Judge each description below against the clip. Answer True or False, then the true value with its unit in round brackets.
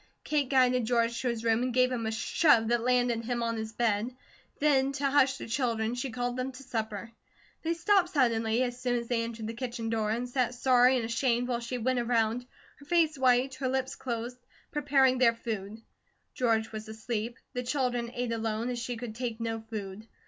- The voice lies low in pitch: False (240 Hz)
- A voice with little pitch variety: True (2.1 semitones)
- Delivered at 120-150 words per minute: False (205 wpm)